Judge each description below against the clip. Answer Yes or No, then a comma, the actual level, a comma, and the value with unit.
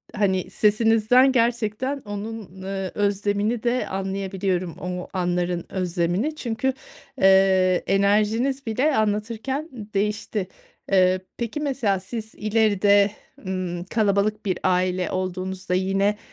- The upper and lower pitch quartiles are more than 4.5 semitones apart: No, average, 3.0 semitones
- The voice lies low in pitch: No, high, 200 Hz